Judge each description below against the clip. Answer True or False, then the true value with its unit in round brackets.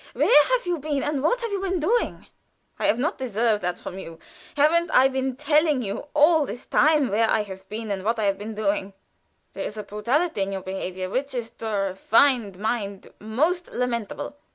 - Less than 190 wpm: False (205 wpm)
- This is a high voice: True (240 Hz)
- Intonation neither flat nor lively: False (6.5 semitones)